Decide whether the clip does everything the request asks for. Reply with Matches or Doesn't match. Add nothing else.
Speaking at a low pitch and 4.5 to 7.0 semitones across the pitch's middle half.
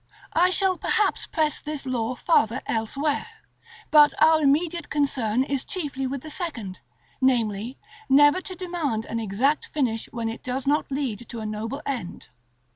Doesn't match